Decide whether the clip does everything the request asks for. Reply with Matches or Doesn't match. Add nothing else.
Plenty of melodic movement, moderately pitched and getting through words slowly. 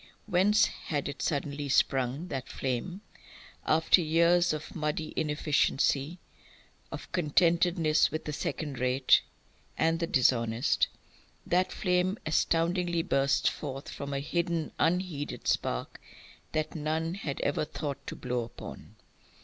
Doesn't match